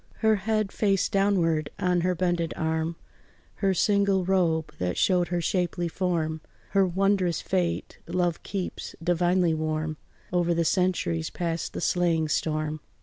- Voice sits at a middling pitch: Yes, medium, 175 Hz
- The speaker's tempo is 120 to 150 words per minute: Yes, average, 140 wpm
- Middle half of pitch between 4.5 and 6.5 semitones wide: No, average, 2.7 semitones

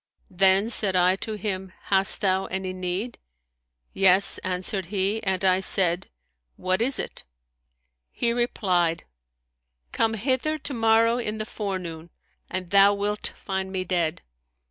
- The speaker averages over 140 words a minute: No, slow, 135 wpm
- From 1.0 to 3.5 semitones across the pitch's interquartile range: Yes, average, 2.7 semitones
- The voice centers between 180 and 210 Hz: Yes, high, 190 Hz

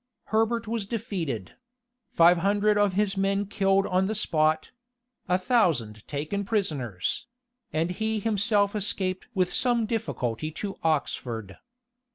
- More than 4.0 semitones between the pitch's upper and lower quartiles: Yes, average, 5.0 semitones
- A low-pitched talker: No, high, 195 Hz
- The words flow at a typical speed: No, slow, 125 wpm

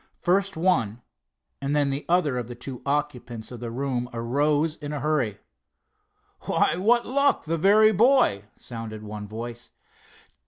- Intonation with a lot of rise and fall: Yes, wide, 6.7 semitones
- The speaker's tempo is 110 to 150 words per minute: Yes, average, 145 wpm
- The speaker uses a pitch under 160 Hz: Yes, medium, 140 Hz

